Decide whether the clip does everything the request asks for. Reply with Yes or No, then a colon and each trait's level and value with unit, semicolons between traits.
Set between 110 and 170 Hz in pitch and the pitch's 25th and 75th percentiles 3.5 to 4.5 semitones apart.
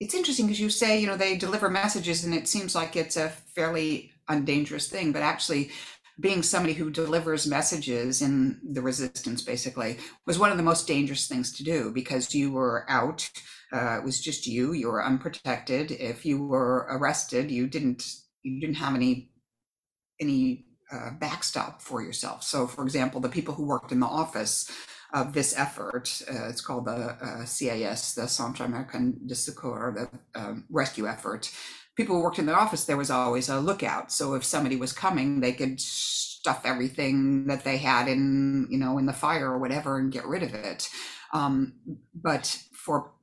Yes: low, 135 Hz; average, 3.9 semitones